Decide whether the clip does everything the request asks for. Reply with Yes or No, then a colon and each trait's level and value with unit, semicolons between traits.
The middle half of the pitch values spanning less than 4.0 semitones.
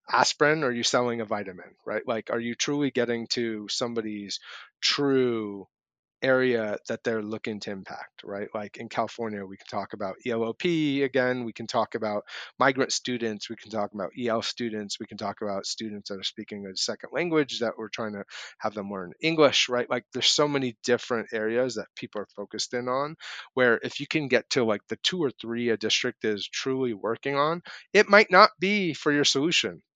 Yes: average, 3.4 semitones